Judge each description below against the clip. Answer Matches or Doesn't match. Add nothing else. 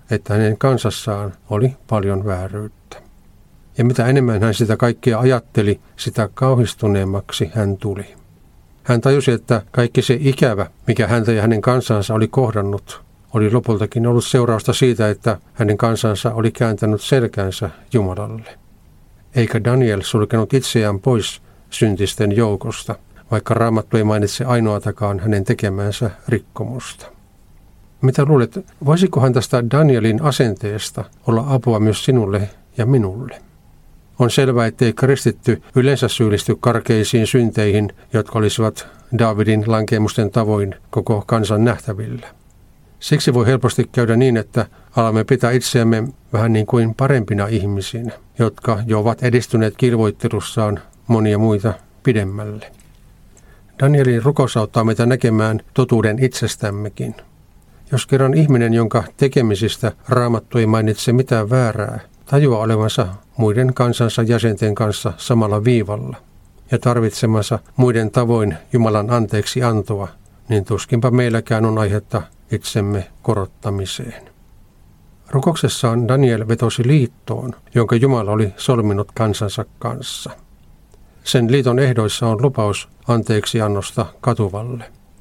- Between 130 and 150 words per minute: Doesn't match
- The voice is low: Matches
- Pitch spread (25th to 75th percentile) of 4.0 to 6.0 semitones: Doesn't match